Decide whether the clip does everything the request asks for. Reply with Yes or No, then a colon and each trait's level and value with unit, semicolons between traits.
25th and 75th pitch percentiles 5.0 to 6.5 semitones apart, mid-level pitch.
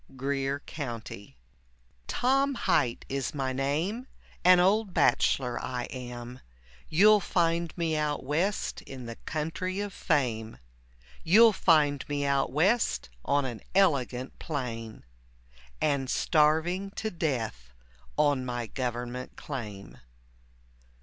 Yes: wide, 5.6 semitones; medium, 145 Hz